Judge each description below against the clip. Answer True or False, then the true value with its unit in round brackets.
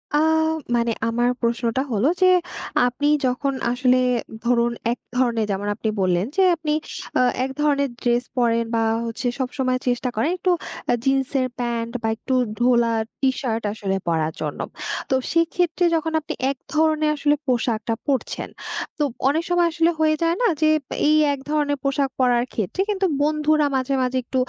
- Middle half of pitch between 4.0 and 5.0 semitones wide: True (4.3 semitones)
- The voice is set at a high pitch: True (255 Hz)